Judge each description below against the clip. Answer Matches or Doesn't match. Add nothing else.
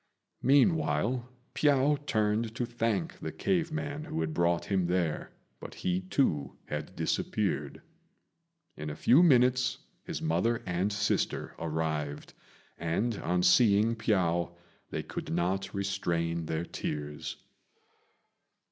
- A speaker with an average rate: Doesn't match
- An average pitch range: Doesn't match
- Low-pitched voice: Matches